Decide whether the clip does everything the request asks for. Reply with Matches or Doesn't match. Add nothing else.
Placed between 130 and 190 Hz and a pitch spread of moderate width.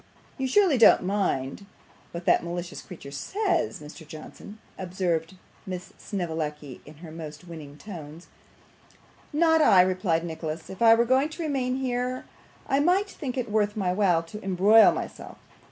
Doesn't match